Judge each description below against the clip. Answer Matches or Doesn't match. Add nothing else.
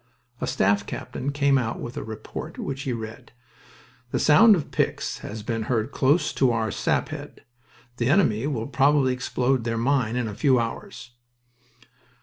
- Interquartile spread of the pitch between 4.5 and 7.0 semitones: Doesn't match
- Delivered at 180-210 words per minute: Doesn't match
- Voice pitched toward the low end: Matches